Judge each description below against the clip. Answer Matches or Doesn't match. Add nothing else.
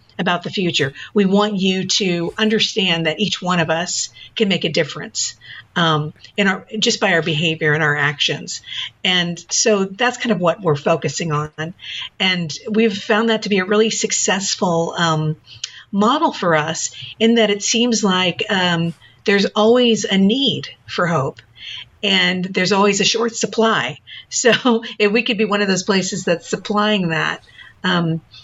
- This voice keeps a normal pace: Matches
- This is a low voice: Doesn't match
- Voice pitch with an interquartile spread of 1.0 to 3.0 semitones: Doesn't match